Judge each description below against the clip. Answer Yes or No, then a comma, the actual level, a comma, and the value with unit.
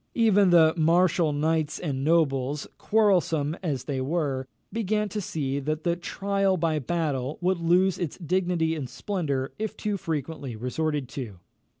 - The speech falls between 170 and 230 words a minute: No, average, 145 wpm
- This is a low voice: No, medium, 160 Hz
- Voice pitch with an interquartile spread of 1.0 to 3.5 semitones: No, average, 4.3 semitones